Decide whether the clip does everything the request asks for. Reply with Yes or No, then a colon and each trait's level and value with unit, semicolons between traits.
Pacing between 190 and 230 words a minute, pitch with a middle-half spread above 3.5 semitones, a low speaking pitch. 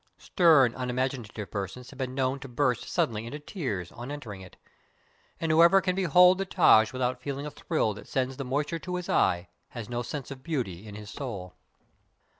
Yes: average, 195 wpm; average, 5.0 semitones; low, 130 Hz